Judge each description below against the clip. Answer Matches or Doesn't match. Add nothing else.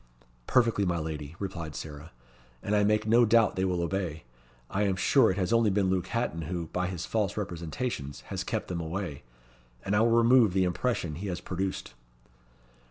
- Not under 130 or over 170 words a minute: Doesn't match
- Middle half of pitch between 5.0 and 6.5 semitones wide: Doesn't match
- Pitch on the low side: Matches